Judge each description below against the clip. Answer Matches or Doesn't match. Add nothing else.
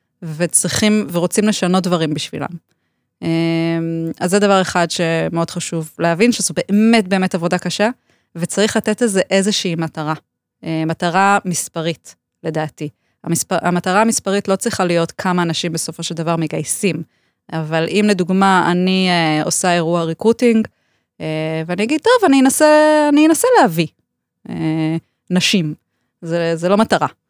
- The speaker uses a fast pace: Doesn't match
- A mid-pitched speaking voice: Matches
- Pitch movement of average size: Matches